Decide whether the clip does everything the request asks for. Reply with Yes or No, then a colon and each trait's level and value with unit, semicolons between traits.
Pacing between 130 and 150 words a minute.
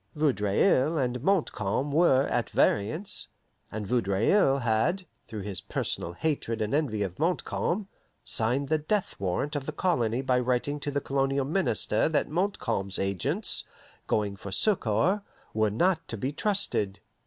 Yes: average, 145 wpm